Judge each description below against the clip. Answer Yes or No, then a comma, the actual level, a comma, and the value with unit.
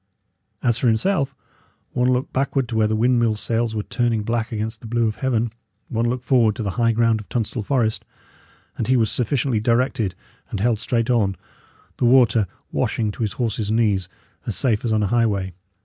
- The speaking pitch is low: Yes, low, 115 Hz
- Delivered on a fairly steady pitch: Yes, narrow, 2.1 semitones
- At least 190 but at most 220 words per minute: Yes, average, 195 wpm